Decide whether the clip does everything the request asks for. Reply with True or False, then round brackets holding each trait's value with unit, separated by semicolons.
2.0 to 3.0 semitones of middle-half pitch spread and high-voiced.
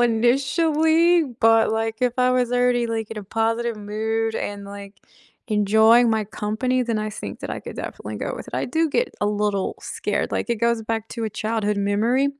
True (2.6 semitones; 225 Hz)